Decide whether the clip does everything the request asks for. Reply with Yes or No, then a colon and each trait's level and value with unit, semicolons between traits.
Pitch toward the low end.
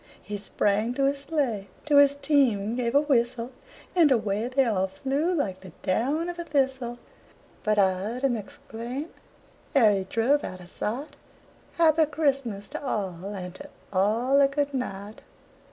No: high, 245 Hz